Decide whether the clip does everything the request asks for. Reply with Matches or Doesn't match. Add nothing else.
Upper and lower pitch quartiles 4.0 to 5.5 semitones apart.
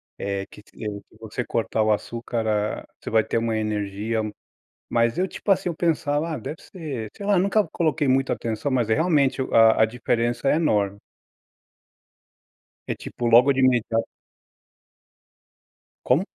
Matches